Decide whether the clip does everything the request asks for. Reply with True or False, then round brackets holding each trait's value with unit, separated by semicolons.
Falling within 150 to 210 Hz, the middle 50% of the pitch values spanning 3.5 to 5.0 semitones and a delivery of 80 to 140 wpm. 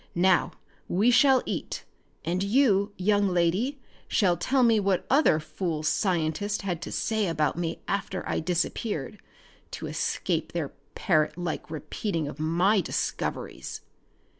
True (185 Hz; 4.0 semitones; 135 wpm)